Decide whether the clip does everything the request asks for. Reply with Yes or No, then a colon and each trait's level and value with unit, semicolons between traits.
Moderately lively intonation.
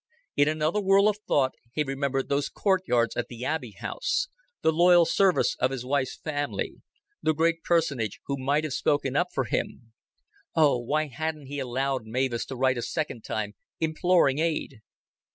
Yes: average, 3.6 semitones